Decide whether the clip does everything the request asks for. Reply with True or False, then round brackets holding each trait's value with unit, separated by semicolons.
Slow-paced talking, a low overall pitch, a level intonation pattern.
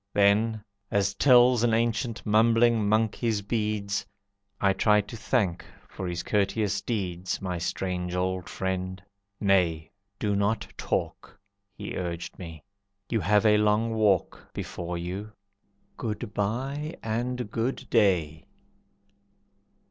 False (120 wpm; 105 Hz; 3.3 semitones)